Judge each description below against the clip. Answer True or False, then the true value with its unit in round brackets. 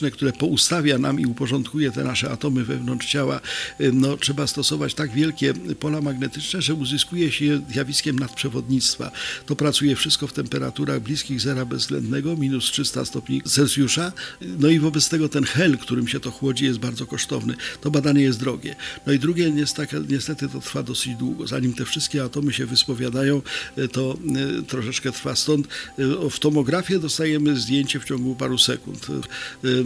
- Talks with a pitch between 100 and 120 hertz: False (140 Hz)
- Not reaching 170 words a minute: True (160 wpm)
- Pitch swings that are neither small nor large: False (2.3 semitones)